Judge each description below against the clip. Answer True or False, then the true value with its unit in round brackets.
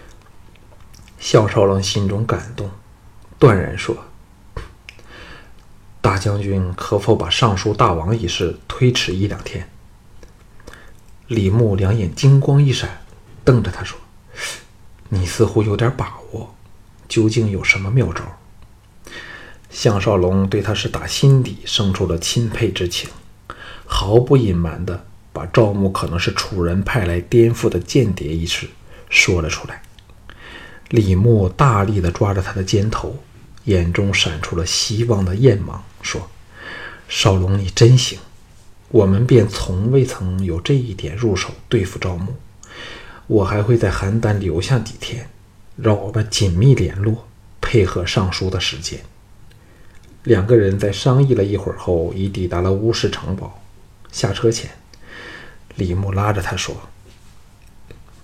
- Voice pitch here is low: True (100 Hz)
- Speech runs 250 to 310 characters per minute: False (195 characters per minute)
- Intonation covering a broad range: False (3.3 semitones)